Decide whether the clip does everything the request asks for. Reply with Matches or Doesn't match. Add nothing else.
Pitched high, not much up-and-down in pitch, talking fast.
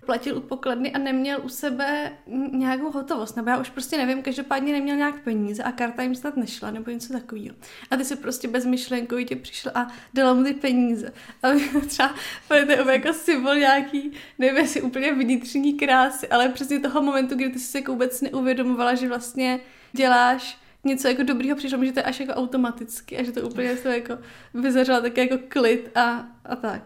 Matches